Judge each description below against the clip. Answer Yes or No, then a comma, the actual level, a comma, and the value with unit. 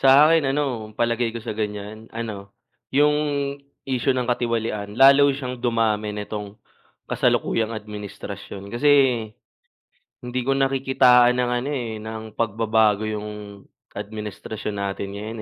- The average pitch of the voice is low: Yes, low, 115 Hz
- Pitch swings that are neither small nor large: Yes, average, 3.3 semitones